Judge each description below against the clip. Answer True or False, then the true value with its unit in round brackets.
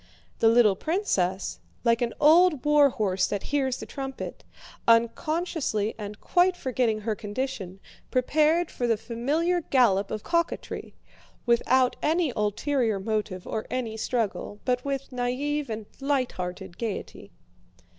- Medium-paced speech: False (125 wpm)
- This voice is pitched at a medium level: False (245 Hz)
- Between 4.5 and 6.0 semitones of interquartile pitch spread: True (5.1 semitones)